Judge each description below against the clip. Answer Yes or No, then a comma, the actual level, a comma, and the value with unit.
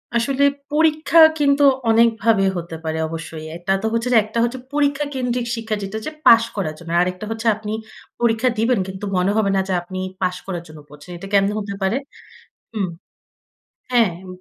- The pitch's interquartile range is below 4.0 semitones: No, average, 4.4 semitones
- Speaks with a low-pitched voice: No, high, 215 Hz